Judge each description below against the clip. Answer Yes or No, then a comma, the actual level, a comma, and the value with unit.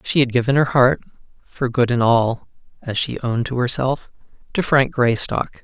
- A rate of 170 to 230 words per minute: No, average, 160 wpm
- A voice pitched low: Yes, low, 125 Hz